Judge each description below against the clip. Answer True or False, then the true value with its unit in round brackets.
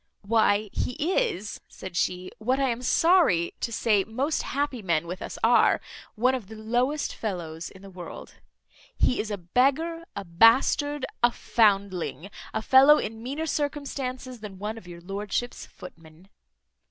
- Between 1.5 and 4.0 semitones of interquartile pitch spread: False (5.6 semitones)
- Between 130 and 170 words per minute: True (155 wpm)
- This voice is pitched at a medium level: False (220 Hz)